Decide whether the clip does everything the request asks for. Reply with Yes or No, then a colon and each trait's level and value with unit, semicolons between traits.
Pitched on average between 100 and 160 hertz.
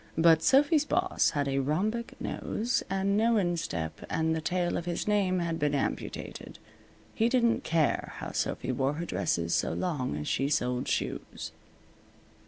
No: medium, 170 Hz